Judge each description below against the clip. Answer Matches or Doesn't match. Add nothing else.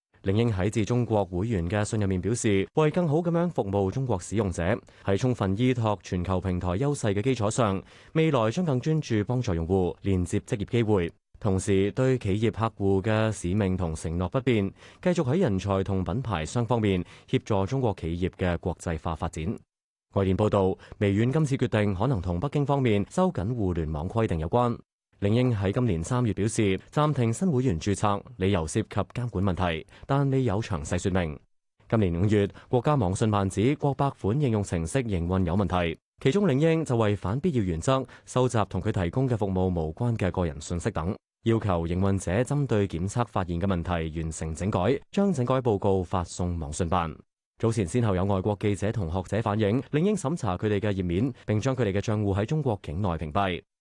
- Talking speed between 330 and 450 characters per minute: Doesn't match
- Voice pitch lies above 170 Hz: Doesn't match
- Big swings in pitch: Doesn't match